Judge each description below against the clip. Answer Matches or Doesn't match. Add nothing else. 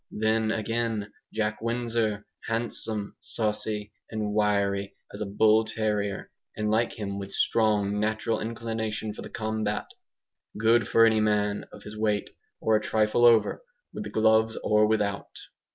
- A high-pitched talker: Doesn't match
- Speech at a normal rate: Matches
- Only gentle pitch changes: Matches